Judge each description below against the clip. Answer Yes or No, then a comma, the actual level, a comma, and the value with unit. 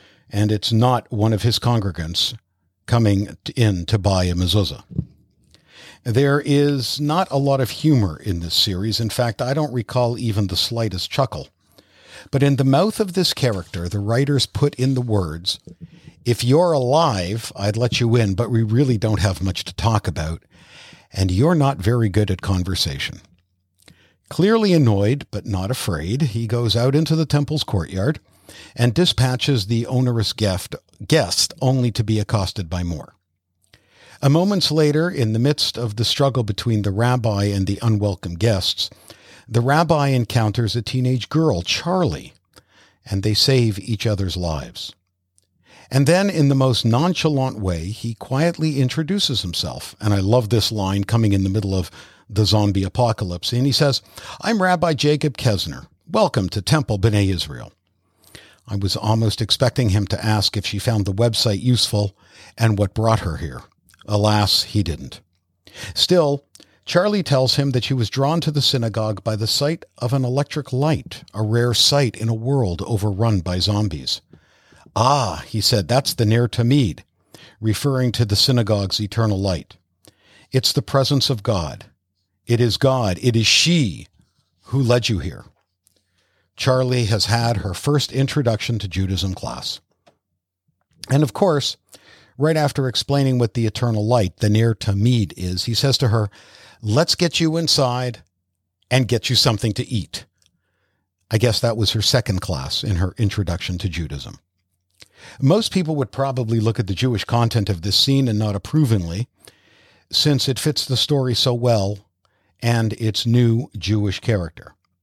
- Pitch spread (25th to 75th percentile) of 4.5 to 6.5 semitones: Yes, average, 4.8 semitones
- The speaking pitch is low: Yes, low, 115 Hz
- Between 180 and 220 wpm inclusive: No, average, 160 wpm